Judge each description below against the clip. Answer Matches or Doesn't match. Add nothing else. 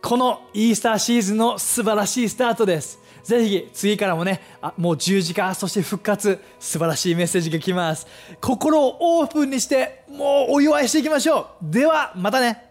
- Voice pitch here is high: Matches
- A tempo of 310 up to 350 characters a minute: Doesn't match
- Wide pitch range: Matches